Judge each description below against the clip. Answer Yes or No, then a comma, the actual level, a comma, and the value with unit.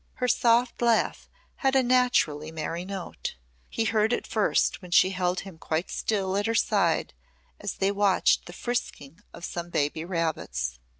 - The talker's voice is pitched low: No, high, 190 Hz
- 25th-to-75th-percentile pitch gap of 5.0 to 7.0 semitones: Yes, average, 5.3 semitones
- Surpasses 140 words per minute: Yes, average, 165 wpm